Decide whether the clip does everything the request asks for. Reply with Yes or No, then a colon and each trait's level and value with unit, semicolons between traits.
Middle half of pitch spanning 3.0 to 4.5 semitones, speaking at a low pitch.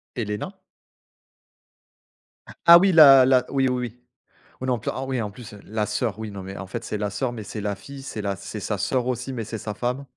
Yes: average, 3.9 semitones; low, 115 Hz